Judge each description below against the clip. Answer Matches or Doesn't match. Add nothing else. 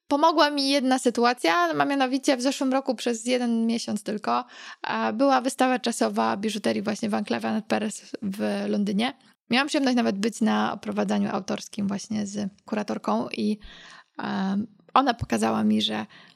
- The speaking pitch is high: Matches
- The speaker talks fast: Doesn't match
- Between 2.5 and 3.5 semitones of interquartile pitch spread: Doesn't match